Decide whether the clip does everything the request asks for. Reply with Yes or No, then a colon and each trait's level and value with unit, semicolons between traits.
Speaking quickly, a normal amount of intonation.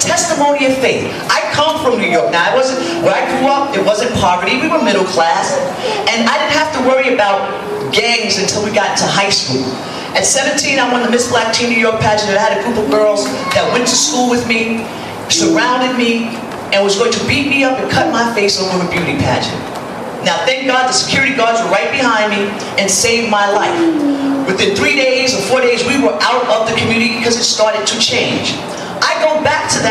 Yes: fast, 215 wpm; average, 4.0 semitones